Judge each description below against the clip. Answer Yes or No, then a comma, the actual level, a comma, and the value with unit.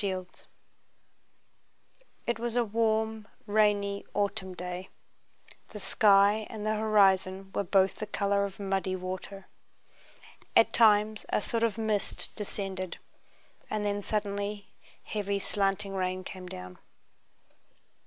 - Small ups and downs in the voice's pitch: Yes, narrow, 1.9 semitones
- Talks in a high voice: Yes, high, 200 Hz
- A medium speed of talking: No, slow, 120 wpm